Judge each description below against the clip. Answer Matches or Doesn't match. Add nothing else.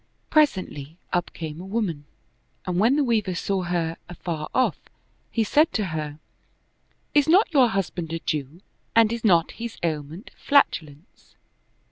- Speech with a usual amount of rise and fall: Doesn't match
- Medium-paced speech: Matches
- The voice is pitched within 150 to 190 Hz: Matches